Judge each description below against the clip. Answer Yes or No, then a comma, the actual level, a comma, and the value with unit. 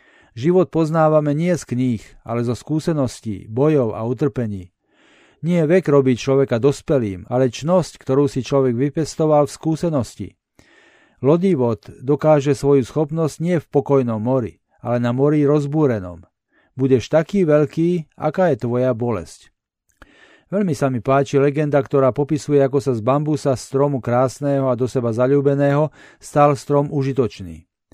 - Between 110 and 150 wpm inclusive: Yes, average, 135 wpm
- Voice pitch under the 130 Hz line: No, medium, 140 Hz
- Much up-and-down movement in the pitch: No, average, 3.3 semitones